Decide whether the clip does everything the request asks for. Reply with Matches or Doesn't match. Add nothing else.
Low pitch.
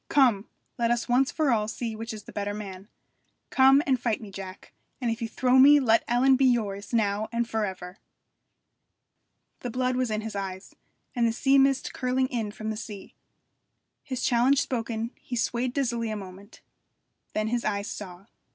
Doesn't match